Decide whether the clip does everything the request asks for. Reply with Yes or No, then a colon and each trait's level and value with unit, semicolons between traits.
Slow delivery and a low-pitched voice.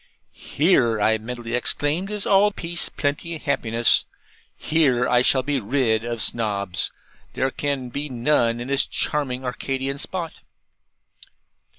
Yes: slow, 125 wpm; low, 130 Hz